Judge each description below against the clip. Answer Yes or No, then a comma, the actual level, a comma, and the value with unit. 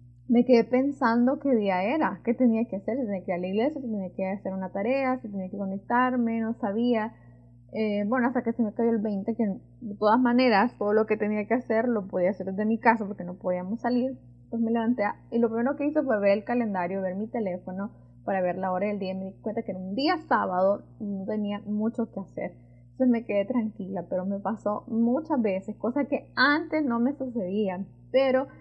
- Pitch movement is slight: No, average, 3.8 semitones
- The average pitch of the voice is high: Yes, high, 215 Hz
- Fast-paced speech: Yes, fast, 230 wpm